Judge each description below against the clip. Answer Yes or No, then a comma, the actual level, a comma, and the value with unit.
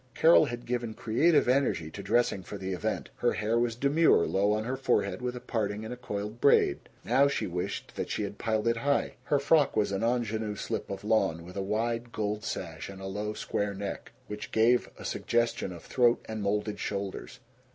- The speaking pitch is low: Yes, low, 110 Hz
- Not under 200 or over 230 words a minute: Yes, fast, 205 wpm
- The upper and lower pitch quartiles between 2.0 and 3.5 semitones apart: Yes, average, 3.2 semitones